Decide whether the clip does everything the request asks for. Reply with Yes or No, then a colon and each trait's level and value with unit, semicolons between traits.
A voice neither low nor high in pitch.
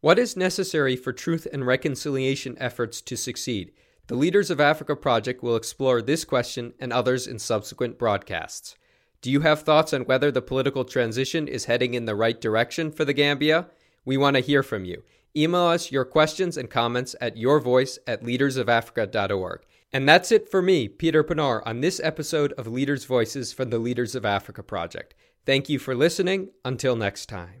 No: low, 130 Hz